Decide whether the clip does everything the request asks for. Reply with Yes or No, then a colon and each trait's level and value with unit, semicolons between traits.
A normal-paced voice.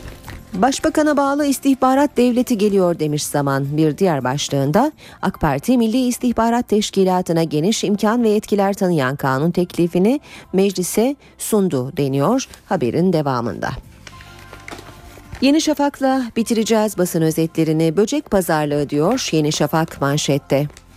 Yes: average, 110 wpm